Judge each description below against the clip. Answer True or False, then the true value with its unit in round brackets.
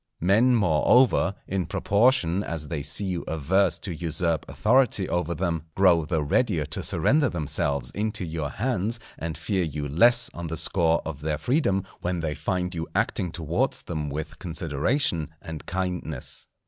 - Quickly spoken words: False (160 wpm)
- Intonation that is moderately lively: True (3.9 semitones)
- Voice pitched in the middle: False (85 Hz)